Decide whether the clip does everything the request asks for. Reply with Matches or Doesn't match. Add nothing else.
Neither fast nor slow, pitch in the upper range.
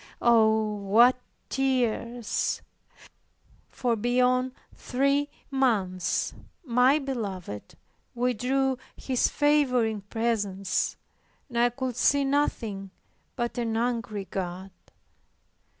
Doesn't match